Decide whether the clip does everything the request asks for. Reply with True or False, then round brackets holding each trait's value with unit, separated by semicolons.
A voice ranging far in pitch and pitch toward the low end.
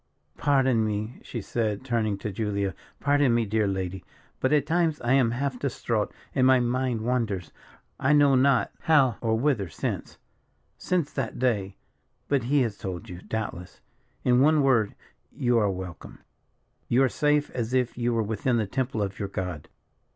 False (4.3 semitones; 120 Hz)